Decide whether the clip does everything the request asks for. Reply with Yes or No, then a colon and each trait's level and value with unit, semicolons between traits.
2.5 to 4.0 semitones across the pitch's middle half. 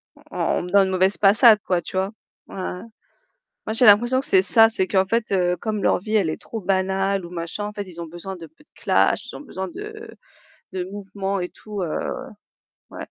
Yes: average, 2.8 semitones